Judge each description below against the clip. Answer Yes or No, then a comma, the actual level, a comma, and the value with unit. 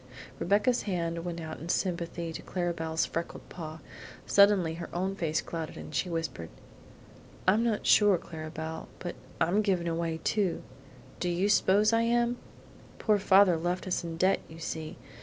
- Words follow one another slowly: No, average, 160 wpm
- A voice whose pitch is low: No, medium, 175 Hz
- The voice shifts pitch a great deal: No, average, 3.4 semitones